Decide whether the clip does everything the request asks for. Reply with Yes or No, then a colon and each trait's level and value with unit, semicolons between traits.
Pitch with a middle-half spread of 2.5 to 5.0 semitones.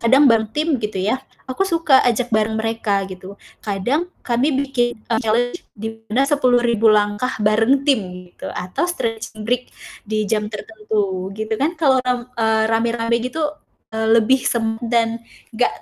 Yes: average, 2.9 semitones